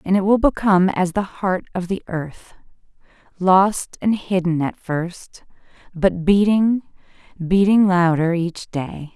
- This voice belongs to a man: No, female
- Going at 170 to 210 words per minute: No, average, 140 wpm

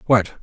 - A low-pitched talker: Yes, low, 110 Hz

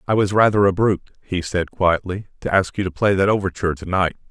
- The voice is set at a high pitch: No, very low, 95 Hz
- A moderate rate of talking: No, fast, 235 wpm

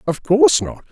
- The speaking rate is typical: Yes, average, 195 wpm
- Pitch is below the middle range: No, medium, 165 Hz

